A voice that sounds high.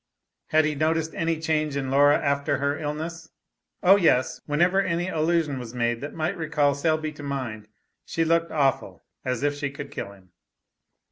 No: medium, 150 Hz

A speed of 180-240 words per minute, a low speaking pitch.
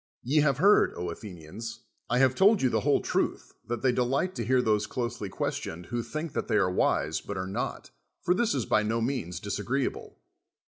Yes: average, 195 wpm; low, 120 Hz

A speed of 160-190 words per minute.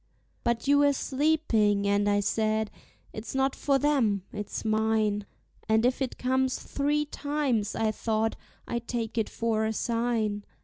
No: average, 150 wpm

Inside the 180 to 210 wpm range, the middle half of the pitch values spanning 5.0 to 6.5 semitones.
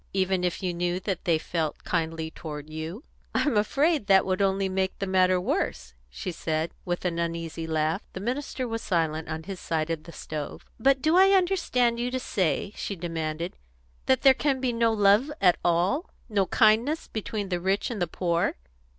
Yes: average, 190 wpm; wide, 5.5 semitones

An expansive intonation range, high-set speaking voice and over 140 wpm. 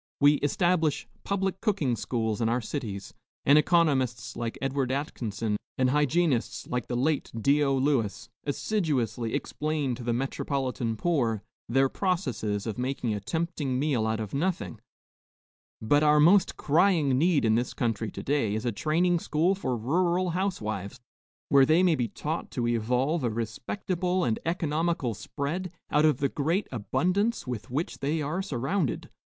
No: wide, 5.8 semitones; medium, 140 Hz; average, 155 wpm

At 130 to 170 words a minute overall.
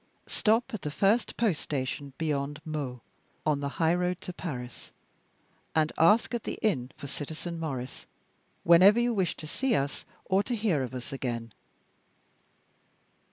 Yes: average, 155 wpm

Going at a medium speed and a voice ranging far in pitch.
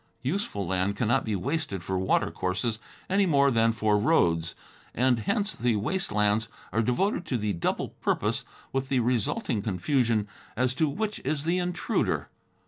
Yes: average, 155 wpm; wide, 6.4 semitones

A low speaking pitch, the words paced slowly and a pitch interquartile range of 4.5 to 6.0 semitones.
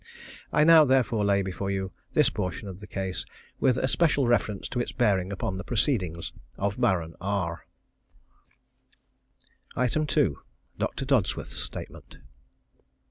Yes: low, 100 Hz; slow, 125 wpm; average, 5.1 semitones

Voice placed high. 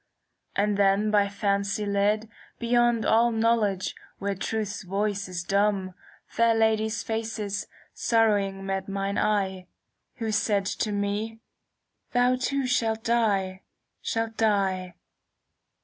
Yes: high, 210 Hz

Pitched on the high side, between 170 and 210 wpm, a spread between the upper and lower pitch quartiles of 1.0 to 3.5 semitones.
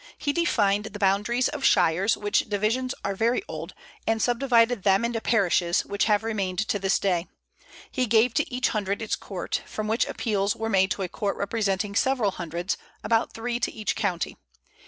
Yes: high, 210 Hz; average, 180 wpm; average, 3.0 semitones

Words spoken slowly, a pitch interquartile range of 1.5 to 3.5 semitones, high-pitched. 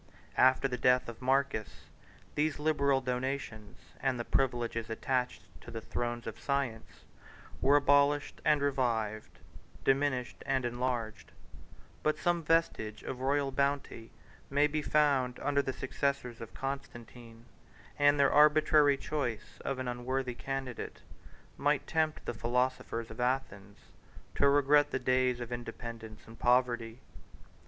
No: slow, 130 wpm; average, 2.9 semitones; low, 130 Hz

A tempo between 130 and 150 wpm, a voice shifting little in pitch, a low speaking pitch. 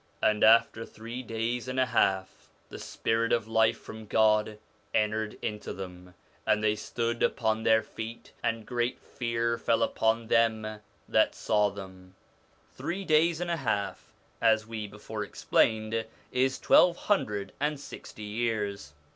Yes: average, 145 wpm; narrow, 1.7 semitones; low, 110 Hz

